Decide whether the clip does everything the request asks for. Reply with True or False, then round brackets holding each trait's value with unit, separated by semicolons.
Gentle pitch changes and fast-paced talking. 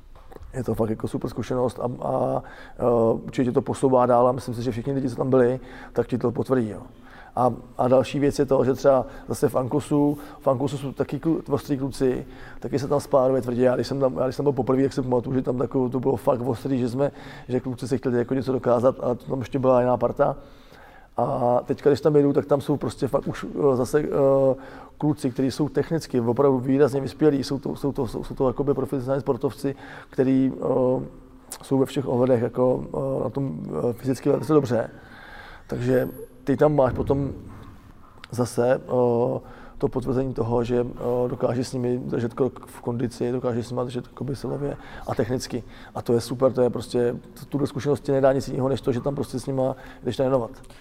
True (1.8 semitones; 205 wpm)